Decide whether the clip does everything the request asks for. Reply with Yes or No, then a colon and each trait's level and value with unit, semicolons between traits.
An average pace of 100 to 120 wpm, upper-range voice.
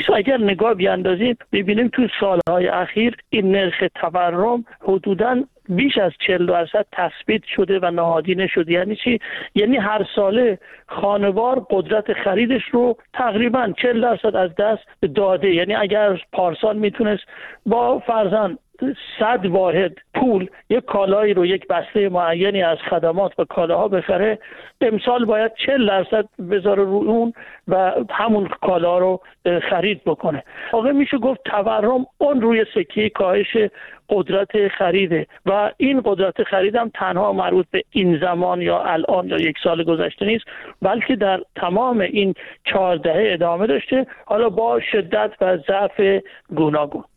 No: average, 140 wpm; high, 205 Hz